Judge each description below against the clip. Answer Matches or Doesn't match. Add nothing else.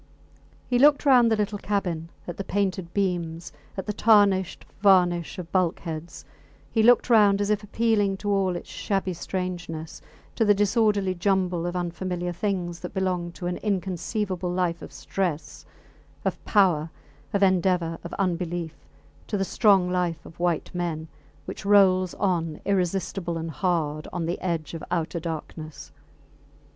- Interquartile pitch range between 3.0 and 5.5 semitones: Doesn't match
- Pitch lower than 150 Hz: Doesn't match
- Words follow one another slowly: Doesn't match